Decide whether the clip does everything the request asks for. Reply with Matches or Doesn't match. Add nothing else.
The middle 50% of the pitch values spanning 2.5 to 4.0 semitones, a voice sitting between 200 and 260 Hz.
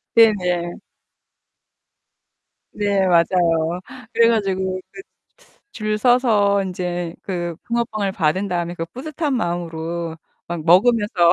Doesn't match